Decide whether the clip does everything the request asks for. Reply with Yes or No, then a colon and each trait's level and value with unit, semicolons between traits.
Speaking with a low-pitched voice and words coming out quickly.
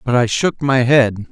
Yes: low, 130 Hz; fast, 230 wpm